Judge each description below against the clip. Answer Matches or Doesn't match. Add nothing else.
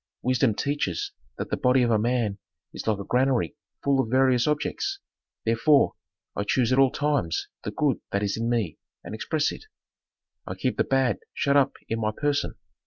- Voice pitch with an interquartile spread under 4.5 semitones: Matches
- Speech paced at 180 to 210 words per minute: Matches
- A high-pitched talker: Doesn't match